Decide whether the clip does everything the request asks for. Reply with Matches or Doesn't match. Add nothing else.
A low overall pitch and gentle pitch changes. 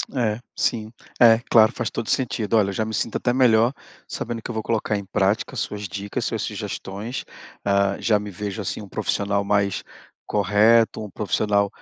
Matches